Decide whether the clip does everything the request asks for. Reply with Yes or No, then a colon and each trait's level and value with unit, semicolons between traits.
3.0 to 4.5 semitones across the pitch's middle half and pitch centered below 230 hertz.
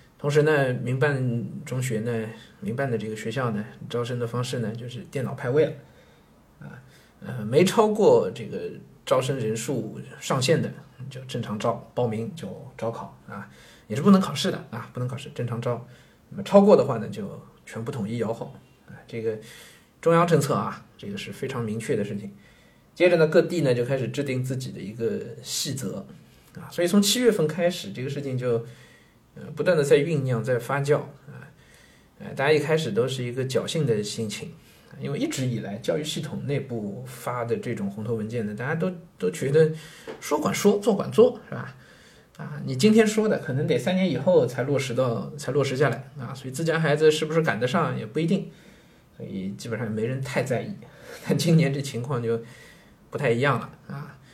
No: average, 5.3 semitones; low, 135 Hz